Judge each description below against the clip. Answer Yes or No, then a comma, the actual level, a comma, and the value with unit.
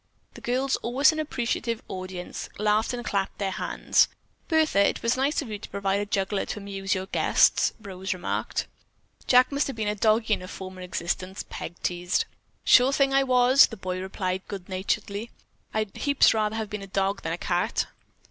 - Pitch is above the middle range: Yes, high, 205 Hz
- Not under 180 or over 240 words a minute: Yes, average, 190 wpm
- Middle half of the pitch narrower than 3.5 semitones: No, average, 4.3 semitones